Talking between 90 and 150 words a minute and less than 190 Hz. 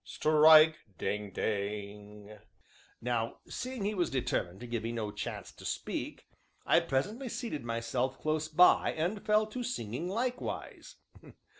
Yes: slow, 135 wpm; low, 135 Hz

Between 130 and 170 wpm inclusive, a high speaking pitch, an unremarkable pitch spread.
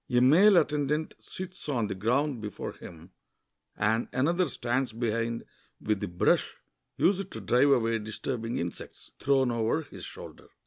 No: average, 145 wpm; low, 120 Hz; average, 4.8 semitones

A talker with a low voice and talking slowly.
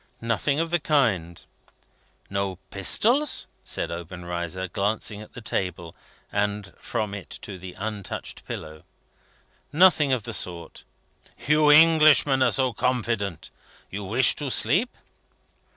Yes: low, 105 Hz; slow, 120 wpm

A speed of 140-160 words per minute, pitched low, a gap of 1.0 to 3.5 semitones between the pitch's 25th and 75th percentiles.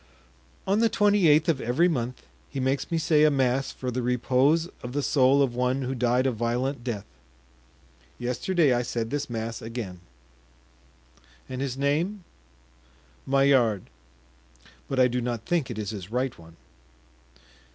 Yes: average, 155 wpm; low, 130 Hz; average, 3.0 semitones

